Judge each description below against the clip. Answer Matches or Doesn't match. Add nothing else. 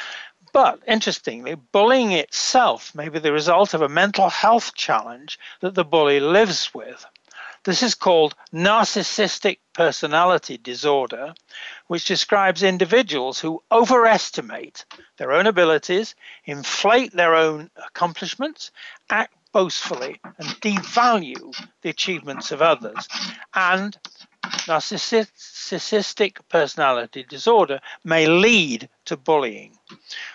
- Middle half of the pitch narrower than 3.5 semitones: Doesn't match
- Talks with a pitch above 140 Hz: Matches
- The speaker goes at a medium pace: Doesn't match